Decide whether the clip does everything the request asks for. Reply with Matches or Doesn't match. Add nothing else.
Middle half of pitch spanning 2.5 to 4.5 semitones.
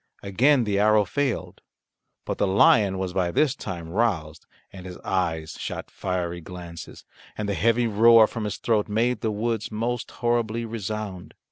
Matches